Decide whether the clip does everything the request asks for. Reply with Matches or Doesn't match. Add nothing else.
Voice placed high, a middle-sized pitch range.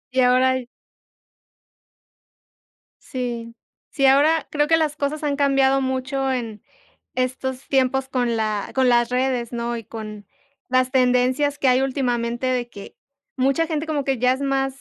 Doesn't match